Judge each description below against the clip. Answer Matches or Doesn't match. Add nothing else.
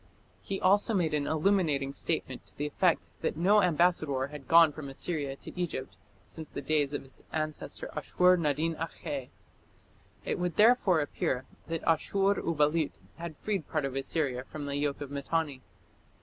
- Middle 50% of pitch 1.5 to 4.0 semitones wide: Matches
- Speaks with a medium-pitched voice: Matches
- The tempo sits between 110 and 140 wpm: Doesn't match